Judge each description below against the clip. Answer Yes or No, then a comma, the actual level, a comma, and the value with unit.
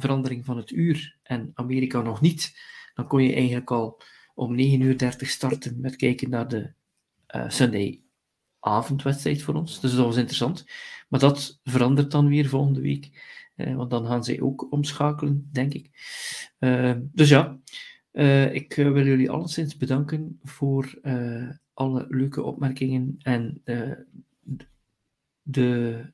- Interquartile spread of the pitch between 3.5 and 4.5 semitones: No, narrow, 2.5 semitones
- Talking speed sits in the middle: Yes, average, 150 wpm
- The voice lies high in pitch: No, low, 135 Hz